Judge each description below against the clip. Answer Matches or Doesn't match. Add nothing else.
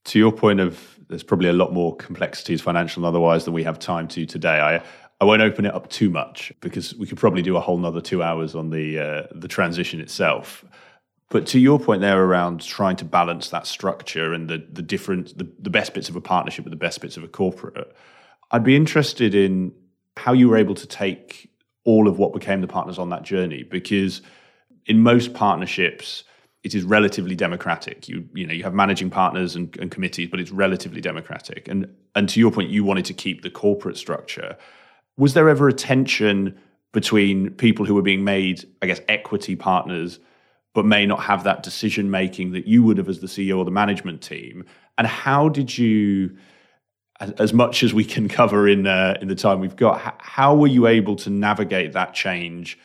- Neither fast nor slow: Doesn't match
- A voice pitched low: Matches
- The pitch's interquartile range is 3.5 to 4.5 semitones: Doesn't match